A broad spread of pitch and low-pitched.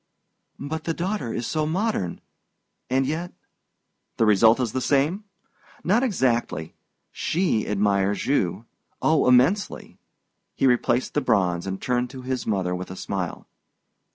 Yes: wide, 7.5 semitones; low, 125 Hz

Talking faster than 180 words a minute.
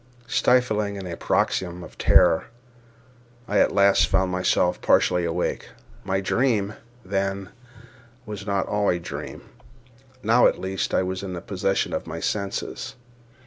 No: average, 140 wpm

